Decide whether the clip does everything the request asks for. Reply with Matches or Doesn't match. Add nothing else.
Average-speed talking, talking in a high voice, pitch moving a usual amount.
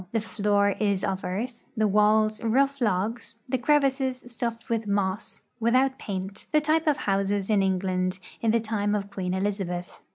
Matches